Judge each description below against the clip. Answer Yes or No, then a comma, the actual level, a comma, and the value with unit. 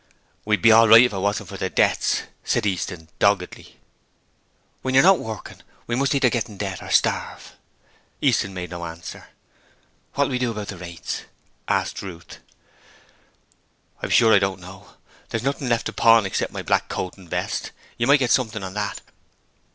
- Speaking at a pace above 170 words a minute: Yes, average, 180 wpm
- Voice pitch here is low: Yes, low, 105 Hz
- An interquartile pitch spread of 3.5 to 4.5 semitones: Yes, average, 4.0 semitones